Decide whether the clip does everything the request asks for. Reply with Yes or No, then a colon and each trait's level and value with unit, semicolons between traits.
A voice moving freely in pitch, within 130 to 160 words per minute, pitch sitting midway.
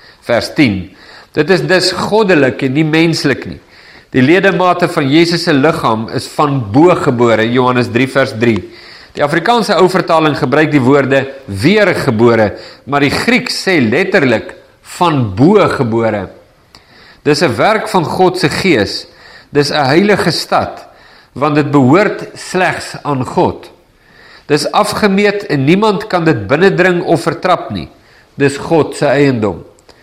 No: average, 5.0 semitones; average, 140 wpm; medium, 150 Hz